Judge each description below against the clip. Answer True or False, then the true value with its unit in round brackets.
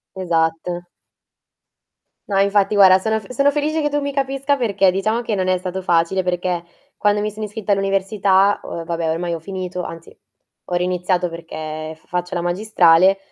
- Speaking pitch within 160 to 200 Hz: True (190 Hz)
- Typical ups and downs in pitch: True (3.1 semitones)